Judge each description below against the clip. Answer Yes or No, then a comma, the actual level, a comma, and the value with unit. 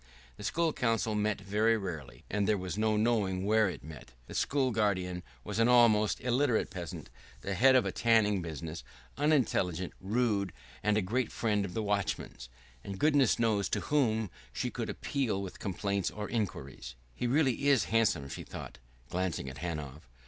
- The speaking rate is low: No, average, 170 wpm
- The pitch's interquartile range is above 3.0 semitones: Yes, average, 4.1 semitones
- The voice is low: Yes, low, 105 Hz